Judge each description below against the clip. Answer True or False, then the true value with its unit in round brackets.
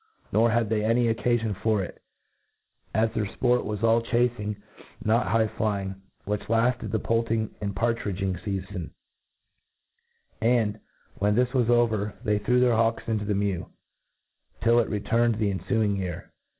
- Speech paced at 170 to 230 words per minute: False (150 wpm)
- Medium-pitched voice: False (110 Hz)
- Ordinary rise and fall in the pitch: False (2.2 semitones)